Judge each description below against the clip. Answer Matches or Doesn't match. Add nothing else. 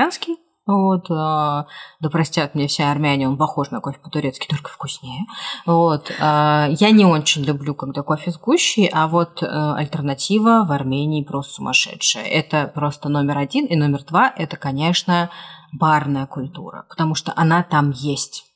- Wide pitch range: Doesn't match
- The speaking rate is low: Doesn't match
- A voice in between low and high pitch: Matches